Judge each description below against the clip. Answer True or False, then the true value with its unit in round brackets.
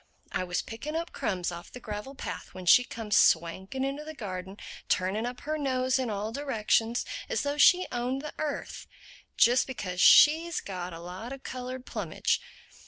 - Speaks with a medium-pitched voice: False (245 Hz)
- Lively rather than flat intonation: True (6.3 semitones)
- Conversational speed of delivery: True (170 wpm)